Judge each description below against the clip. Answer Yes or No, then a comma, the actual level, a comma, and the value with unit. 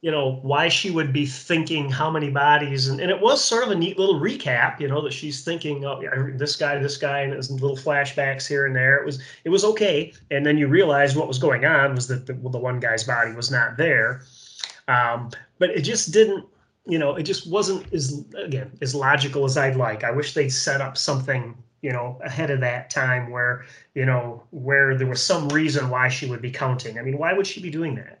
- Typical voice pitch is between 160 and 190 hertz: No, medium, 140 Hz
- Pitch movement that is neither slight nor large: Yes, average, 3.0 semitones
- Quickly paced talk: Yes, fast, 235 wpm